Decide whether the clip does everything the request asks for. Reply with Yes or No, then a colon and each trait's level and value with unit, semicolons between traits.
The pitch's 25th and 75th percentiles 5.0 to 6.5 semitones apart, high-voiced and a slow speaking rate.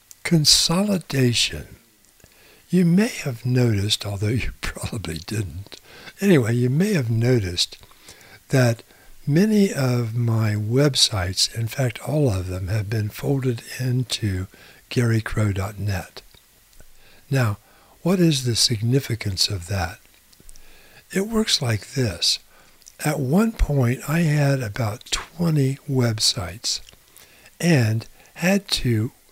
No: average, 5.3 semitones; low, 120 Hz; slow, 105 wpm